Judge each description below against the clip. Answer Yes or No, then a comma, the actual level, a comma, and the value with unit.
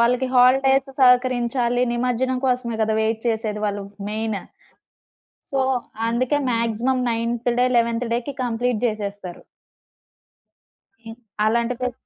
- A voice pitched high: Yes, high, 235 Hz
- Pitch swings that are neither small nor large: No, narrow, 1.9 semitones